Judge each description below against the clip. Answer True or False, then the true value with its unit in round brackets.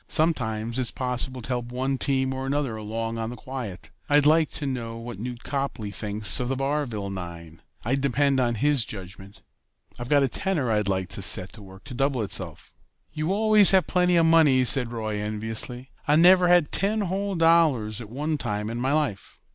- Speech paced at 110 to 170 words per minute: False (195 wpm)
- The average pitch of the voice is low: True (125 Hz)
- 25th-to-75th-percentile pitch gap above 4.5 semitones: True (5.2 semitones)